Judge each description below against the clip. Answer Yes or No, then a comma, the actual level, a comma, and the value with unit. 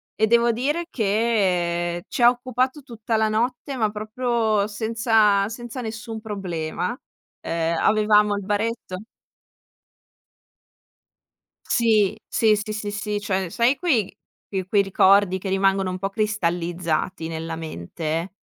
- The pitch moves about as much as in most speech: Yes, average, 3.3 semitones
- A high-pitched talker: Yes, high, 210 Hz